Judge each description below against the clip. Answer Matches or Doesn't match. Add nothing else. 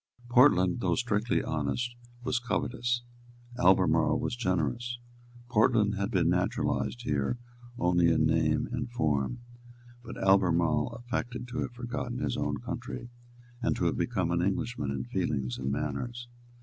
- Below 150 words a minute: Matches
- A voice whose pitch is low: Matches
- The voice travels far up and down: Matches